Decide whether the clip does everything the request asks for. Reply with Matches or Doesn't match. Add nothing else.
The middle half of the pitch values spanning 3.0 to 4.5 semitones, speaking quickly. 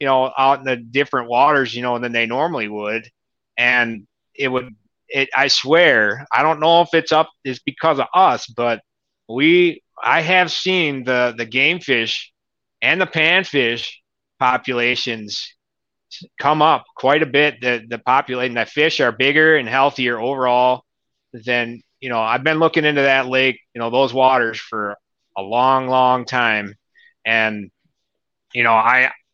Doesn't match